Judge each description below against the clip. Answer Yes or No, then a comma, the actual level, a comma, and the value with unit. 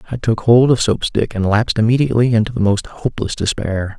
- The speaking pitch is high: No, low, 115 Hz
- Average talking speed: No, fast, 210 wpm